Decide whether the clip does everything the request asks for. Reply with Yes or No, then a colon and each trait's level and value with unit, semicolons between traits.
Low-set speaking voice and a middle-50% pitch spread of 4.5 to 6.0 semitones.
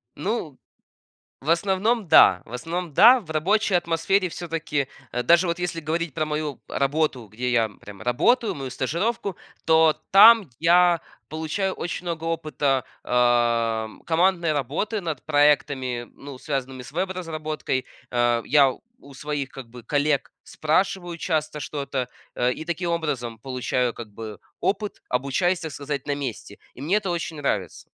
No: medium, 150 Hz; average, 5.0 semitones